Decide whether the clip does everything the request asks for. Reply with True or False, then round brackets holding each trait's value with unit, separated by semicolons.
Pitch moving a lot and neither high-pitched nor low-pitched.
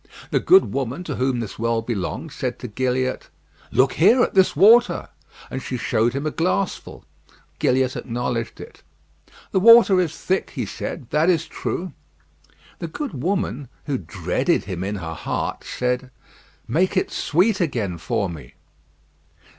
False (7.5 semitones; 130 Hz)